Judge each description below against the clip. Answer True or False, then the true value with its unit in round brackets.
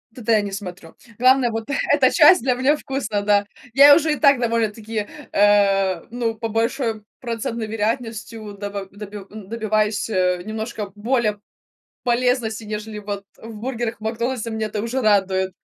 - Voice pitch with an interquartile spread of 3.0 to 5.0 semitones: False (2.5 semitones)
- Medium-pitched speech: False (220 Hz)